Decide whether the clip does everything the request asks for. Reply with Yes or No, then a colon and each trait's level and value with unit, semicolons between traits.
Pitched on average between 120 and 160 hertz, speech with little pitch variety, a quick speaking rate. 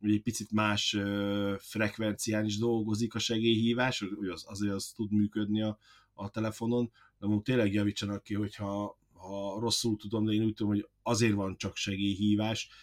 No: low, 105 Hz; narrow, 1.6 semitones; fast, 170 wpm